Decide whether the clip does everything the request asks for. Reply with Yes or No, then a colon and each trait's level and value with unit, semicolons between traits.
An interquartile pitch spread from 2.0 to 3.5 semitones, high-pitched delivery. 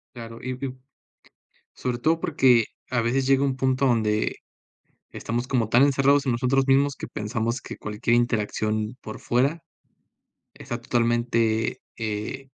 No: average, 2.8 semitones; low, 120 Hz